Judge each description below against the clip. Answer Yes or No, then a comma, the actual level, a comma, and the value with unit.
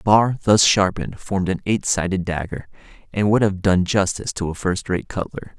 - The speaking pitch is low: Yes, very low, 95 Hz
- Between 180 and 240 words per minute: Yes, fast, 205 wpm